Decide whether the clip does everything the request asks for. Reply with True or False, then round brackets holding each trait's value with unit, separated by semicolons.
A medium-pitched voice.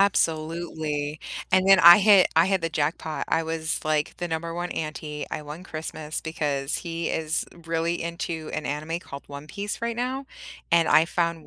True (165 Hz)